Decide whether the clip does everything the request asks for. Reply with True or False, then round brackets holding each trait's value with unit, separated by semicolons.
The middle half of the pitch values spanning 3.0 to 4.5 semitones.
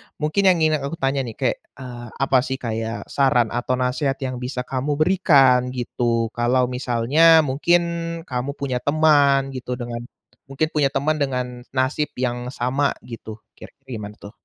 False (2.6 semitones)